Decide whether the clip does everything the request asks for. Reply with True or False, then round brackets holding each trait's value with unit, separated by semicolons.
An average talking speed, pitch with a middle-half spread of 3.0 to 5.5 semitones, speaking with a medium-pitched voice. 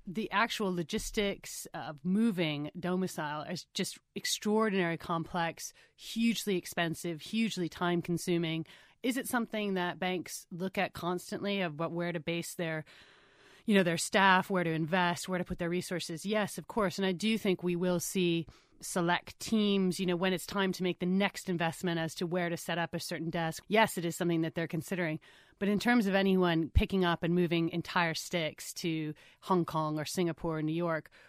False (190 wpm; 2.5 semitones; 180 Hz)